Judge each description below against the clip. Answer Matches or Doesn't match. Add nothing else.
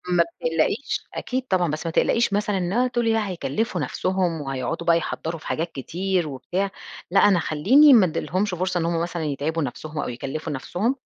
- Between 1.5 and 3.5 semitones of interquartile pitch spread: Doesn't match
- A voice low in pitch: Doesn't match